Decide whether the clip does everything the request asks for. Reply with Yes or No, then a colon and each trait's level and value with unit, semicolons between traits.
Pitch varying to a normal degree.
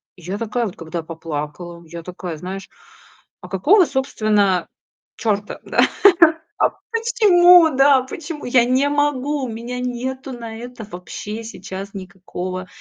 No: wide, 6.4 semitones